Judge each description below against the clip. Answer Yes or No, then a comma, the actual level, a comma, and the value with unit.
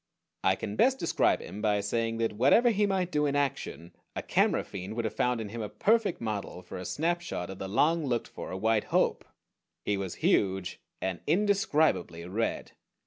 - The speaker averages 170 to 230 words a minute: Yes, average, 190 wpm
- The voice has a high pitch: No, low, 115 Hz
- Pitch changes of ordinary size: No, wide, 8.5 semitones